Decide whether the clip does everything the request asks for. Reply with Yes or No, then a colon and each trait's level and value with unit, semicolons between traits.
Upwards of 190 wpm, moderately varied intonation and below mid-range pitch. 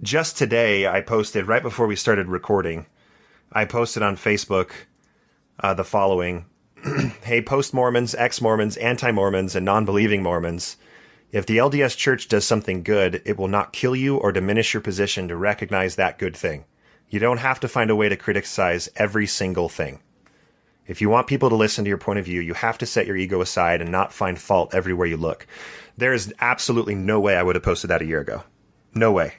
Yes: average, 200 wpm; average, 3.7 semitones; low, 105 Hz